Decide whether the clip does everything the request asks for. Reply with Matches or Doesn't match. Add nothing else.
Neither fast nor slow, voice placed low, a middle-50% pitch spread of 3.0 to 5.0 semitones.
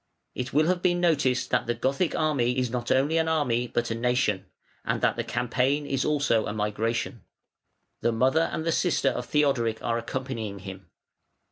Matches